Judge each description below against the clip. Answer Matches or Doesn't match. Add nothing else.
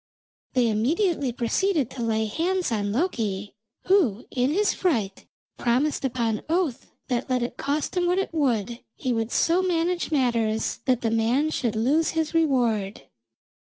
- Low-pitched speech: Doesn't match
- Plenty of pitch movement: Matches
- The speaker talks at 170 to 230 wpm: Doesn't match